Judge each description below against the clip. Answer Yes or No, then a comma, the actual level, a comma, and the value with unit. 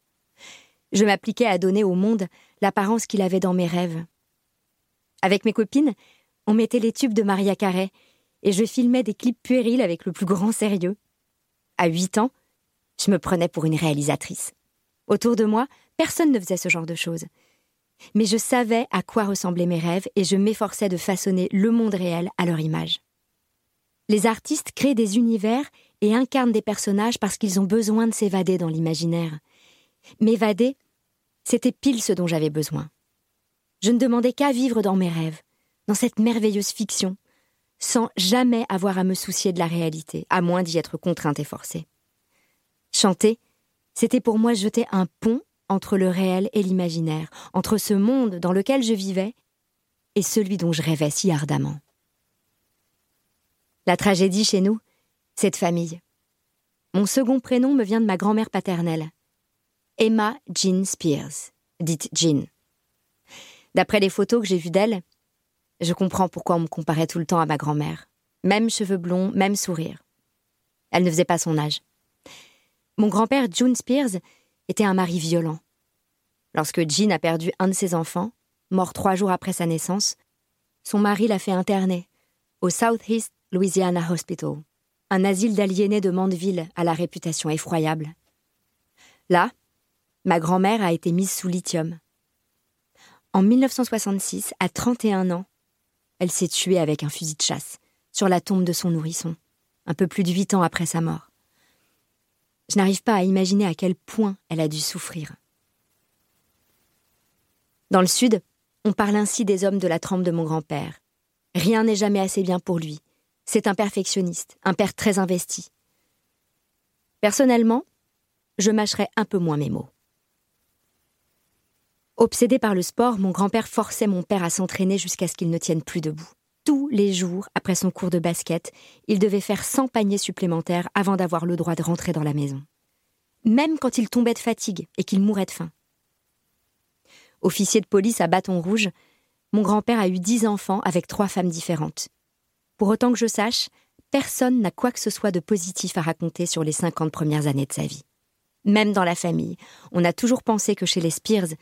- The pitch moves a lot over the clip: No, average, 4.1 semitones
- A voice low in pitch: No, high, 195 Hz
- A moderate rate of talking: Yes, average, 170 wpm